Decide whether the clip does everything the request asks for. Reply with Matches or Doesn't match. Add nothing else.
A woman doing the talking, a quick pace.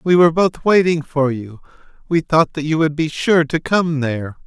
Doesn't match